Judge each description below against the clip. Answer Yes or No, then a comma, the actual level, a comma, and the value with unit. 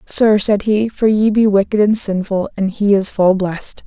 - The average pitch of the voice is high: Yes, high, 205 Hz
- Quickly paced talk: Yes, fast, 215 wpm